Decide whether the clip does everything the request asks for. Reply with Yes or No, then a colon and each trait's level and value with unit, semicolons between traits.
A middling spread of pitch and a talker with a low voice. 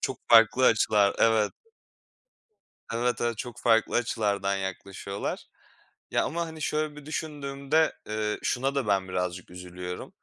No: wide, 5.8 semitones; low, 115 Hz